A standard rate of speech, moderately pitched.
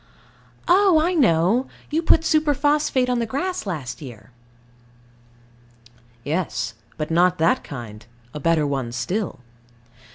No: slow, 120 wpm; medium, 180 Hz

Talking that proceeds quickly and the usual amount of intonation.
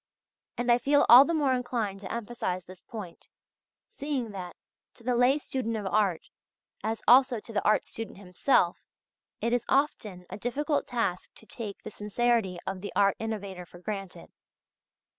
No: average, 165 wpm; average, 4.1 semitones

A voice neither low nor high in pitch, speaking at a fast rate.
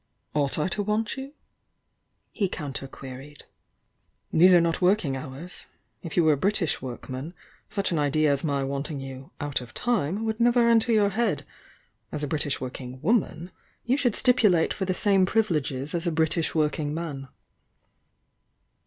No: medium, 160 Hz; average, 165 wpm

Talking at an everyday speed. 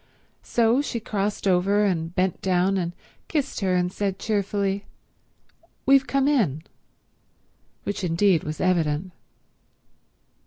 No: slow, 115 wpm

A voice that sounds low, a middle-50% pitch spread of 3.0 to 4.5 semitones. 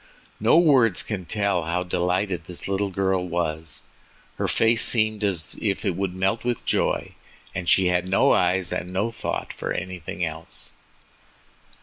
No: very low, 95 Hz; narrow, 2.6 semitones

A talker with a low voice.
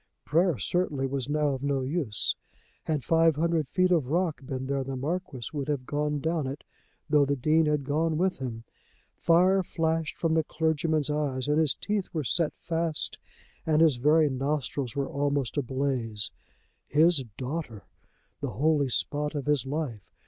No: medium, 150 Hz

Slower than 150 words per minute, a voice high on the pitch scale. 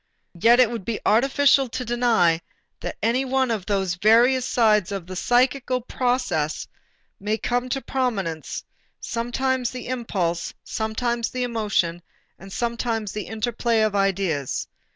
Yes: slow, 135 wpm; high, 230 Hz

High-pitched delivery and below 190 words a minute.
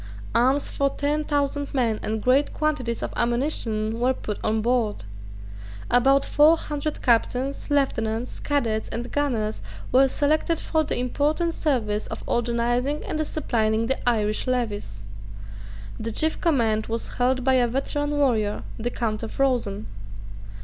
Yes: very high, 250 Hz; average, 140 wpm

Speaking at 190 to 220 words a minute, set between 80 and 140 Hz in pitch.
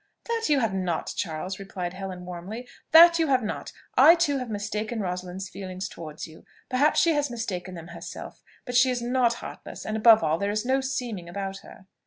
No: average, 200 wpm; high, 210 Hz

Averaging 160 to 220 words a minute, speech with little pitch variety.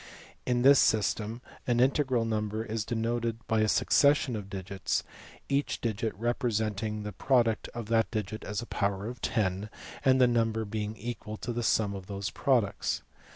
Yes: average, 170 wpm; narrow, 2.3 semitones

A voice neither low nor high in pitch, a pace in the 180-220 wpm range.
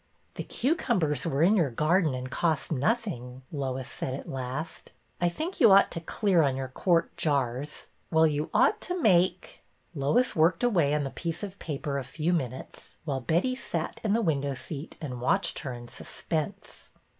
Yes: medium, 155 Hz; average, 195 wpm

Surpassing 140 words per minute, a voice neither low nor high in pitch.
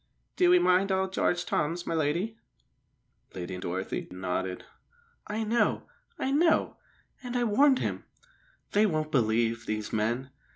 No: slow, 135 wpm; medium, 165 Hz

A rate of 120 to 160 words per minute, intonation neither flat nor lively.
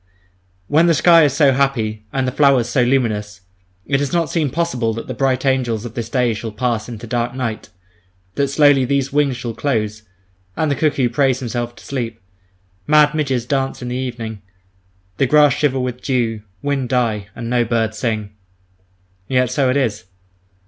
No: average, 180 wpm; average, 3.3 semitones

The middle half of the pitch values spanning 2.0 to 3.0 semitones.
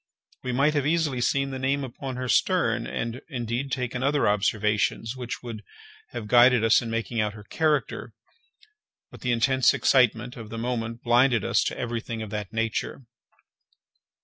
Yes: narrow, 2.6 semitones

